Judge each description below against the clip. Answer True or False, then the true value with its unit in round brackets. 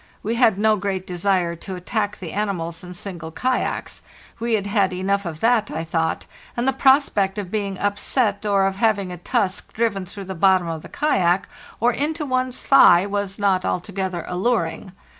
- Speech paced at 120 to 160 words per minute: False (180 wpm)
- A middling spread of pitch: True (3.3 semitones)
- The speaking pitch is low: False (195 Hz)